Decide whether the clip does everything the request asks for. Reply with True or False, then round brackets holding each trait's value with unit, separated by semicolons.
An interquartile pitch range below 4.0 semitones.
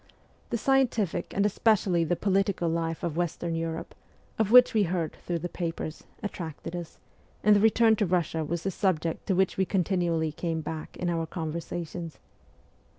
True (3.1 semitones)